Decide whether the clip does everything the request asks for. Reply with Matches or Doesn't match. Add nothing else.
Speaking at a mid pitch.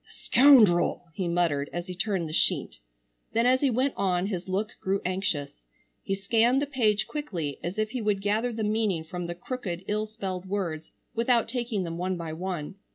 Doesn't match